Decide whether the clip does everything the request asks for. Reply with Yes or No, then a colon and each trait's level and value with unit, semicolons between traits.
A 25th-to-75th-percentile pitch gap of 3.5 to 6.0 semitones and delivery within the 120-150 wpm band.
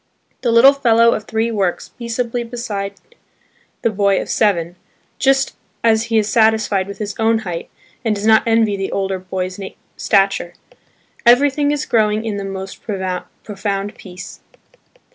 No: average, 3.0 semitones; average, 145 wpm